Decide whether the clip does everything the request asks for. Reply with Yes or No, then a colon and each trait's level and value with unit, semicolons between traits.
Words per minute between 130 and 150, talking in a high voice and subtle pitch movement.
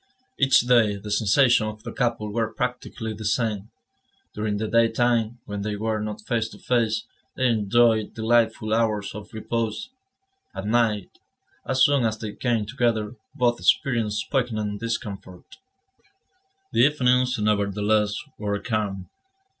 No: slow, 135 wpm; low, 110 Hz; narrow, 2.2 semitones